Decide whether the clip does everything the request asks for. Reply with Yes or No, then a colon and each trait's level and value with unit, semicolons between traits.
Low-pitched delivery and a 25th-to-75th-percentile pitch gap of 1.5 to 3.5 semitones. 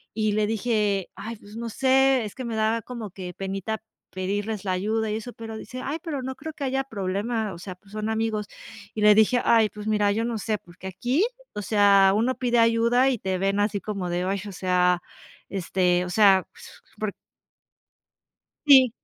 No: high, 215 Hz; average, 3.1 semitones